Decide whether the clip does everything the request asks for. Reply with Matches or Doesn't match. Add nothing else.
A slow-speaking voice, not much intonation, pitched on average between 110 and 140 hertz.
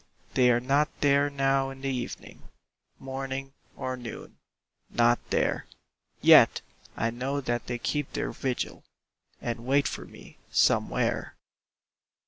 Matches